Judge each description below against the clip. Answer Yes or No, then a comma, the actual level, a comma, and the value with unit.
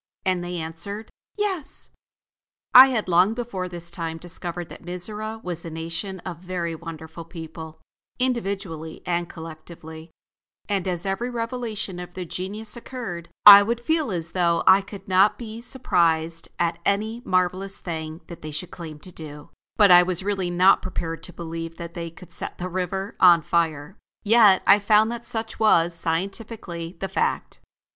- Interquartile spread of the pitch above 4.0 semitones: No, average, 3.6 semitones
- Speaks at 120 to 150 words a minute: No, average, 165 wpm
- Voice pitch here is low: No, medium, 180 Hz